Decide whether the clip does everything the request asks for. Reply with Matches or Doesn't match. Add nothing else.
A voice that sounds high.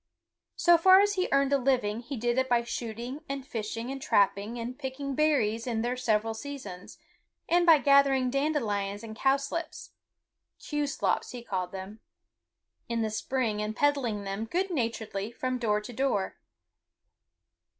Matches